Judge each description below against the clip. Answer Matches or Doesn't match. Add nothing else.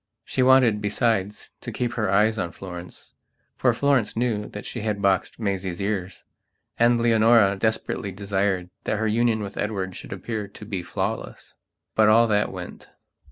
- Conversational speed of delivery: Matches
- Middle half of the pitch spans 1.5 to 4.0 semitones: Matches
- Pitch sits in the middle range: Doesn't match